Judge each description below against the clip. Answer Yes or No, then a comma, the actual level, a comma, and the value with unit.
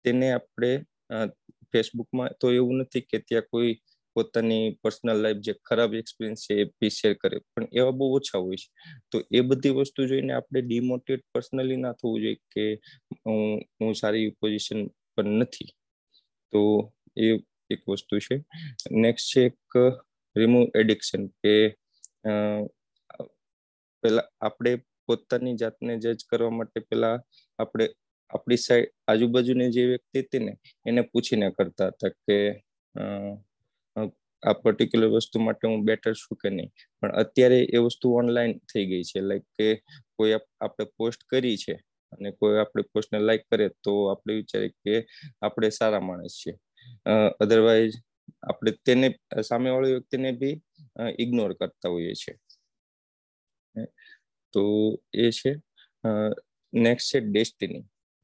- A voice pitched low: Yes, low, 115 Hz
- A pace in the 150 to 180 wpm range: No, slow, 135 wpm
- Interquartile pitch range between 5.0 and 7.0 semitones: No, average, 2.7 semitones